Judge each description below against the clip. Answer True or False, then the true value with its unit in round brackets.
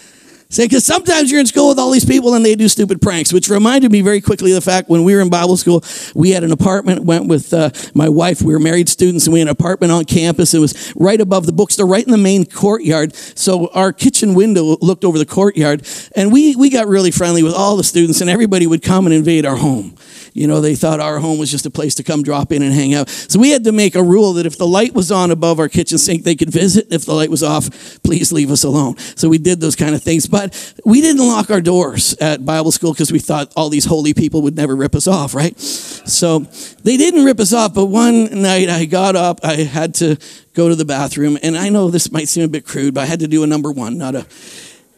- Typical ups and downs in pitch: True (4.0 semitones)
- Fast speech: True (265 wpm)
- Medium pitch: True (170 Hz)